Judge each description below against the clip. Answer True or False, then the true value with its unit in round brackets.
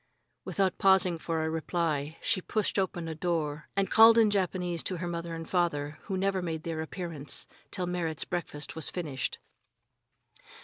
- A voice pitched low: False (170 Hz)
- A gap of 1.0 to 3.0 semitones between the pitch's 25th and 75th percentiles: True (2.7 semitones)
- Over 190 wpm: False (165 wpm)